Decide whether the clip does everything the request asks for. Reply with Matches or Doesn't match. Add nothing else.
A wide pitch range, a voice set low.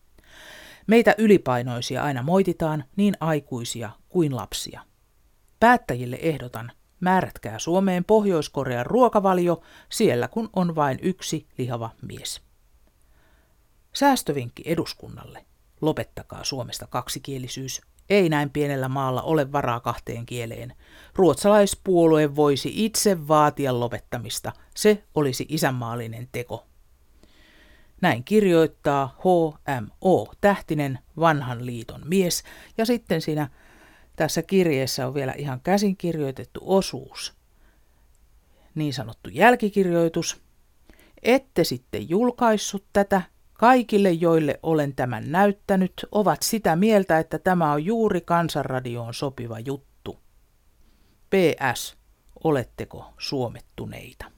Doesn't match